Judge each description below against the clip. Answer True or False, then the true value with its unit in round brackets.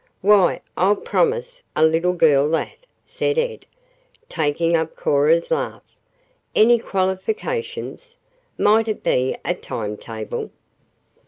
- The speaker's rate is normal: False (110 wpm)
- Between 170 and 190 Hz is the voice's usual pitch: True (185 Hz)